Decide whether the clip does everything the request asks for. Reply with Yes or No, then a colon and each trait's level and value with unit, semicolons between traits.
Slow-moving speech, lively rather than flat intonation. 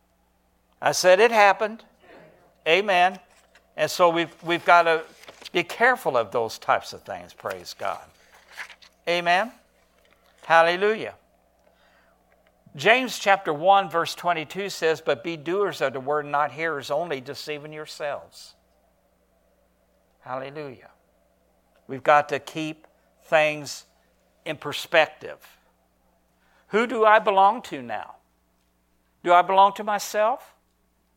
Yes: slow, 110 wpm; wide, 6.1 semitones